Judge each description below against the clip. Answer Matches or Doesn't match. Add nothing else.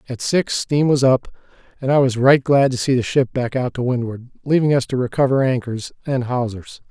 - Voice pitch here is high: Doesn't match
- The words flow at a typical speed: Doesn't match